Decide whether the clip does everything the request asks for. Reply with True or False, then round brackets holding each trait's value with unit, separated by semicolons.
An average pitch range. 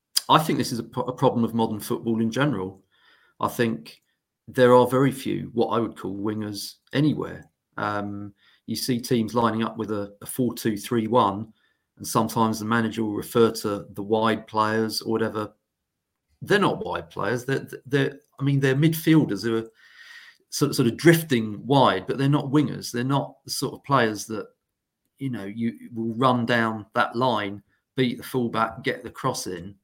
True (3.1 semitones)